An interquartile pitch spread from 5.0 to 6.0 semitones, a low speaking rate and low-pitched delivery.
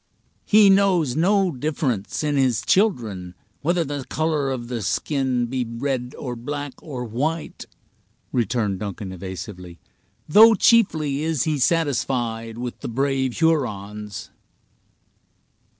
Yes: average, 5.3 semitones; slow, 120 wpm; low, 130 Hz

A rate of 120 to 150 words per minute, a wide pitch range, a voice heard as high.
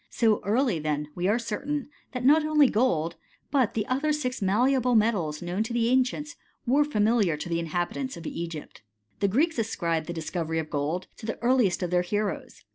No: average, 190 wpm; wide, 7.0 semitones; high, 215 Hz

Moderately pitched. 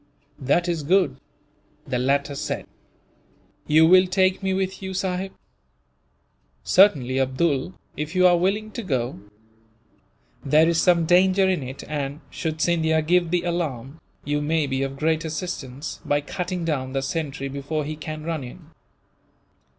Yes: medium, 160 Hz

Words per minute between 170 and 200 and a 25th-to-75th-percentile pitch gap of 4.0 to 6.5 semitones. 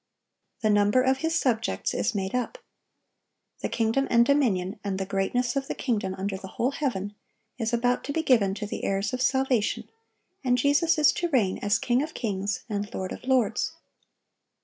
Yes: average, 185 wpm; average, 4.6 semitones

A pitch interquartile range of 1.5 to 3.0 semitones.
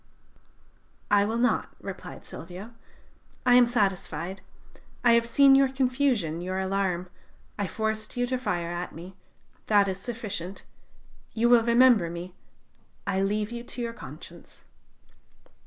No: average, 4.3 semitones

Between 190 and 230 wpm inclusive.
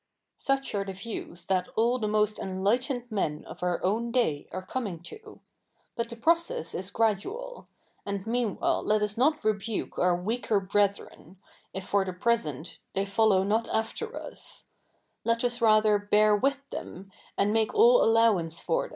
No: average, 175 wpm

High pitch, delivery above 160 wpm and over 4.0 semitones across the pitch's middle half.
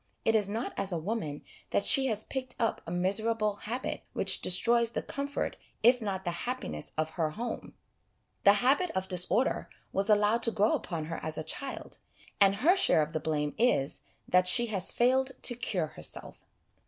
Yes: high, 210 Hz; average, 185 wpm; average, 5.2 semitones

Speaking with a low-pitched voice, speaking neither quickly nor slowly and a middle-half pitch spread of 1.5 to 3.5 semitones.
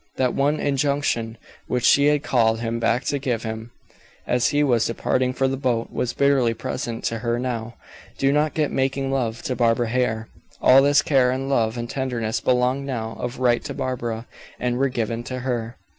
Yes: low, 125 Hz; average, 190 wpm; average, 2.7 semitones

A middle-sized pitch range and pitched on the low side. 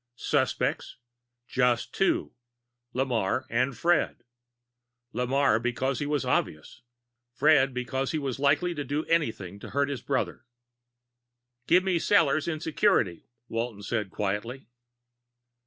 Yes: average, 4.2 semitones; low, 130 Hz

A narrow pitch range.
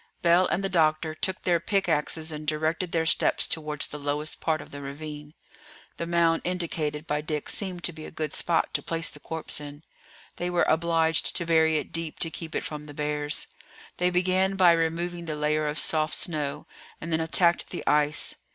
Yes: narrow, 2.2 semitones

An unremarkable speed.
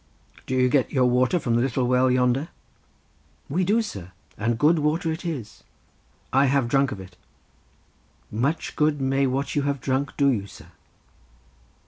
Yes: average, 165 wpm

